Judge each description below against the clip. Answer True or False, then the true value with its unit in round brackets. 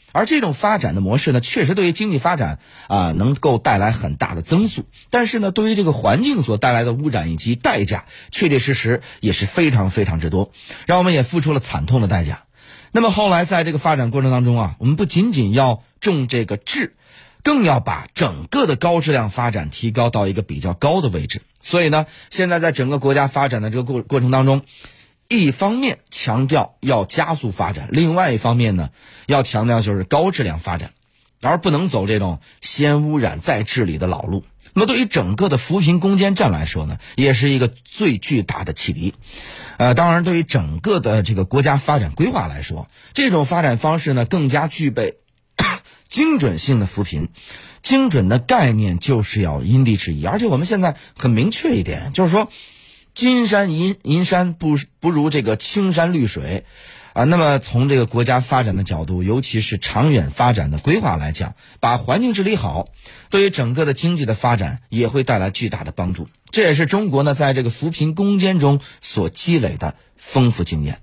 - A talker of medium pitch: False (130 Hz)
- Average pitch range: False (7.6 semitones)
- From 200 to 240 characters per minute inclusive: False (295 characters per minute)